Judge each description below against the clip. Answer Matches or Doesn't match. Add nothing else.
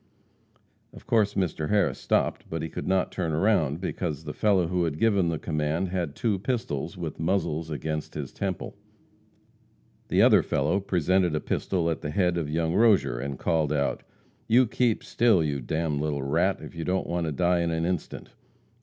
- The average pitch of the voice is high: Doesn't match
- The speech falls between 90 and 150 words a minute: Doesn't match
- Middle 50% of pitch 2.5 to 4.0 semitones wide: Matches